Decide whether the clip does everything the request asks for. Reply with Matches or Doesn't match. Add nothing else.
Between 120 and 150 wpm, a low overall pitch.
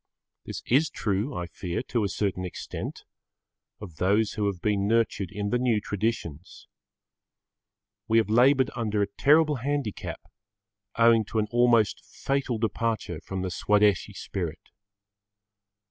Matches